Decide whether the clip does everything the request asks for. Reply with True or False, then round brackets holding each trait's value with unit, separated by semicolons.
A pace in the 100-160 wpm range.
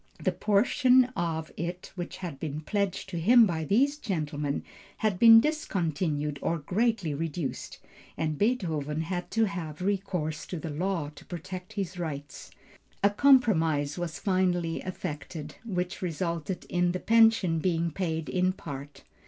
True (145 wpm)